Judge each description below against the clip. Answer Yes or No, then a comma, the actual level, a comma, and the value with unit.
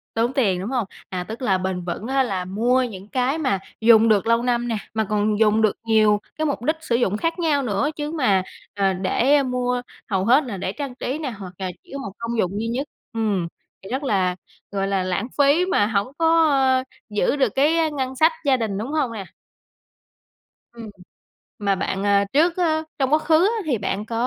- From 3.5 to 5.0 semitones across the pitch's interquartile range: No, wide, 5.5 semitones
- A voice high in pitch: Yes, high, 235 Hz